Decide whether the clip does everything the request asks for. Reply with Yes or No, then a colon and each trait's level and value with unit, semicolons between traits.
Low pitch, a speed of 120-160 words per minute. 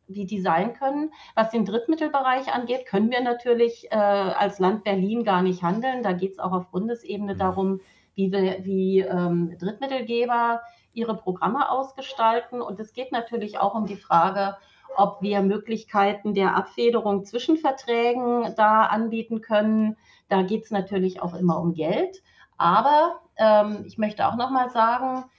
No: high, 215 Hz; average, 155 wpm